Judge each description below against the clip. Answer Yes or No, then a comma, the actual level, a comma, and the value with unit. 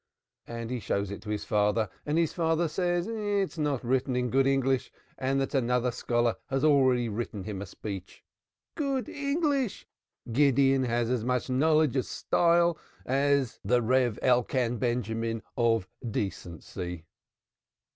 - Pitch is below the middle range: Yes, low, 125 Hz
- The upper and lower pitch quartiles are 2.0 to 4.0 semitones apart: No, average, 4.5 semitones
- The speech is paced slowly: No, average, 145 wpm